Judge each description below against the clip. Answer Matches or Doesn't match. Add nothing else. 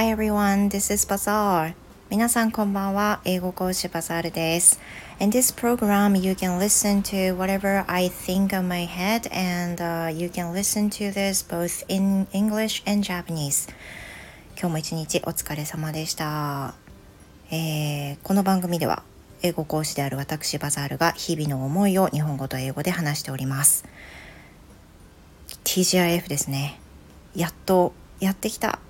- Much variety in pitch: Doesn't match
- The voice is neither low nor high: Matches